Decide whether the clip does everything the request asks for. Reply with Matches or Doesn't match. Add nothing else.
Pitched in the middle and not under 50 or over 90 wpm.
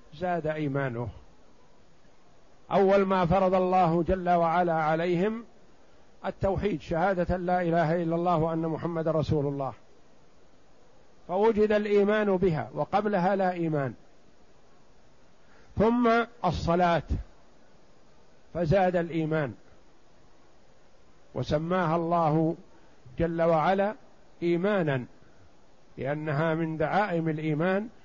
Matches